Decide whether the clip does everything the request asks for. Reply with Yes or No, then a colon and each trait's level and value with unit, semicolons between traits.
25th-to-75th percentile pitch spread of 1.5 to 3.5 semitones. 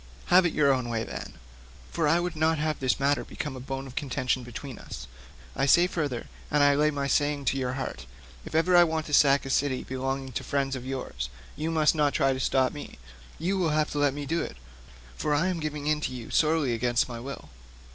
Yes: average, 2.8 semitones